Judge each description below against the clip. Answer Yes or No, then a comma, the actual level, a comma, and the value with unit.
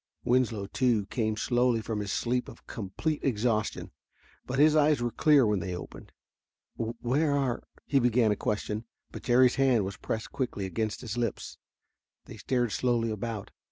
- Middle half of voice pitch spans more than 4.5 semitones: No, average, 3.1 semitones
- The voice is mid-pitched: No, low, 120 Hz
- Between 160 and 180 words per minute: Yes, average, 165 wpm